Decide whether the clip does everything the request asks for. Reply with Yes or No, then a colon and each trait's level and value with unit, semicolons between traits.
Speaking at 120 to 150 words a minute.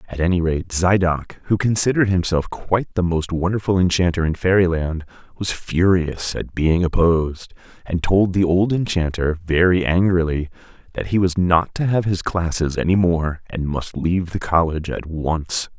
No: average, 165 wpm